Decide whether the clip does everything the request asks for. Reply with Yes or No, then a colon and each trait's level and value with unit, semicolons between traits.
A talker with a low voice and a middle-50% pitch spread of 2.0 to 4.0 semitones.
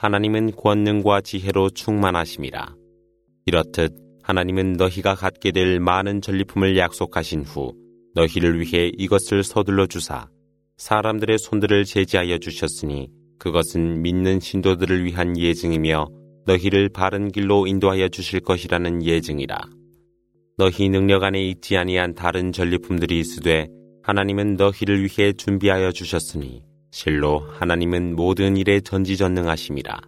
Yes: very low, 95 Hz; average, 2.8 semitones